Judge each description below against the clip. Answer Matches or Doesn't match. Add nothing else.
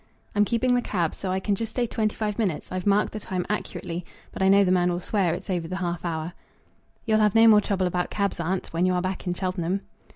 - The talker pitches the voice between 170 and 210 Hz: Matches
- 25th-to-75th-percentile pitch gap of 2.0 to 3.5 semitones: Matches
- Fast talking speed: Matches